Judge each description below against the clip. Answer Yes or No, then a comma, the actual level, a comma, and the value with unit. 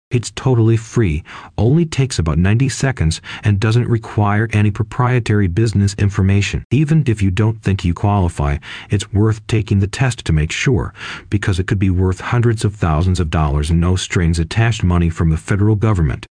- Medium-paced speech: Yes, average, 180 wpm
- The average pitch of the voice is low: Yes, low, 105 Hz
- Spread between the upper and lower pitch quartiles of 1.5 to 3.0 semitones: No, average, 4.0 semitones